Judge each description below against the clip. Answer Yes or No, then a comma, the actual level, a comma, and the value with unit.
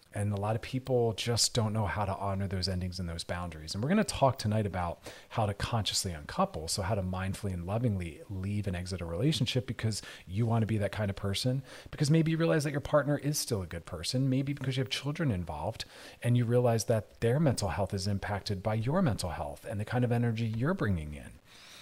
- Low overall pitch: Yes, low, 105 Hz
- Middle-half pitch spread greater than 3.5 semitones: Yes, average, 4.6 semitones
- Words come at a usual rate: No, fast, 235 wpm